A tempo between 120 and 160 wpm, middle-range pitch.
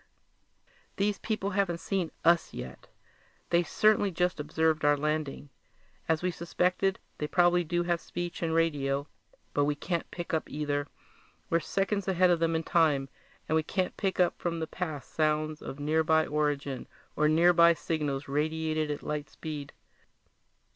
Yes: average, 155 wpm; medium, 160 Hz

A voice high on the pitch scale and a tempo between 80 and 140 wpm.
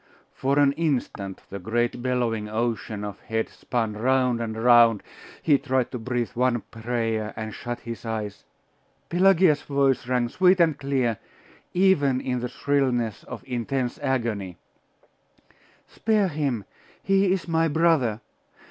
No: low, 125 Hz; slow, 135 wpm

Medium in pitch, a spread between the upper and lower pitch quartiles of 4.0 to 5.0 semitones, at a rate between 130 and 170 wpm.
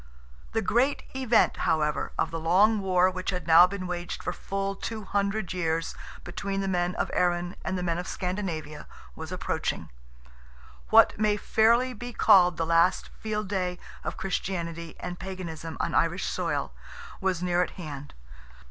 No: medium, 180 Hz; average, 2.8 semitones; average, 160 wpm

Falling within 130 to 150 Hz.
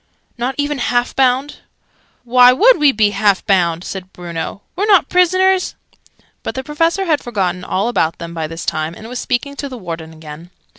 No: high, 240 Hz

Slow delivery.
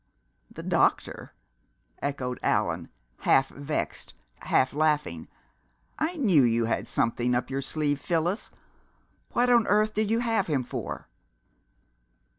Yes: slow, 120 wpm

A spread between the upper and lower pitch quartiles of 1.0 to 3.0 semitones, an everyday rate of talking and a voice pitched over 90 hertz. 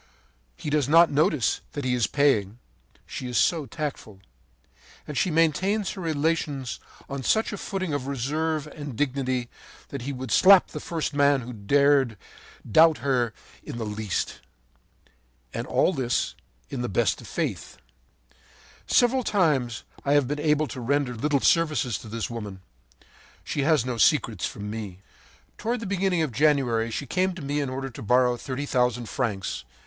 No: average, 4.3 semitones; average, 165 wpm; medium, 140 Hz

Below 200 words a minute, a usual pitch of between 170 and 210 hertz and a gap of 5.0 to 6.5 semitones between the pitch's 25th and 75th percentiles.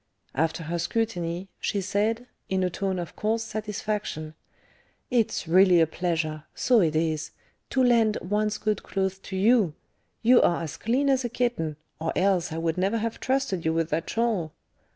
Yes: average, 175 wpm; high, 190 Hz; average, 5.3 semitones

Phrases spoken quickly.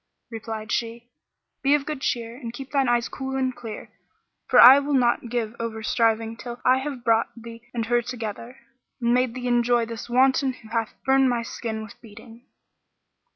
No: average, 185 wpm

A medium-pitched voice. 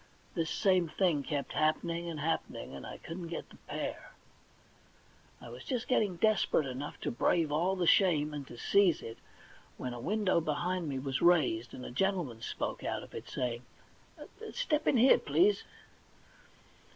Yes: medium, 165 Hz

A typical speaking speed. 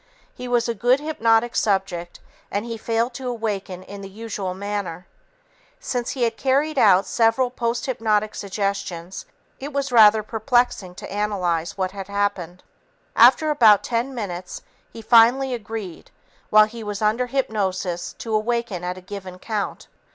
Yes: average, 150 wpm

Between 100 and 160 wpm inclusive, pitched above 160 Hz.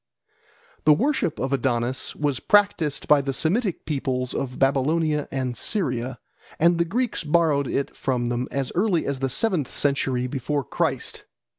No: average, 150 wpm; medium, 140 Hz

